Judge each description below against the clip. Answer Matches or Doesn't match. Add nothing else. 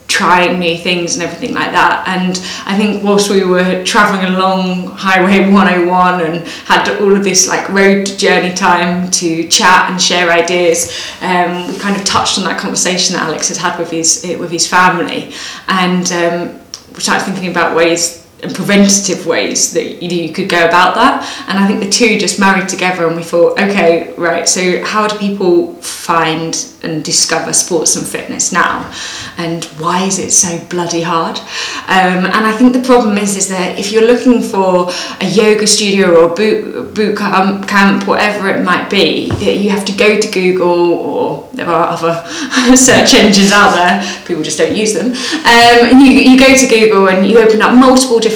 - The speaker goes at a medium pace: Matches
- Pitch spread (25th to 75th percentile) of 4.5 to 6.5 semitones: Doesn't match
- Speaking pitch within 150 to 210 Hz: Matches